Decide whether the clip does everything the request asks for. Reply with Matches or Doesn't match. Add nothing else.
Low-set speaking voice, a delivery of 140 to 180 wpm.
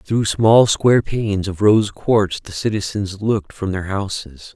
Matches